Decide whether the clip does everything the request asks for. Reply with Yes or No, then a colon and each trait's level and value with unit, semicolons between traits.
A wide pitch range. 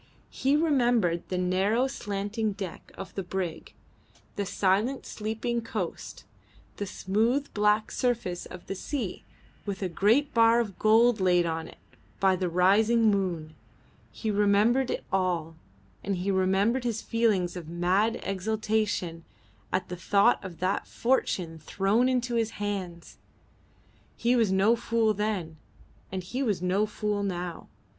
No: average, 3.8 semitones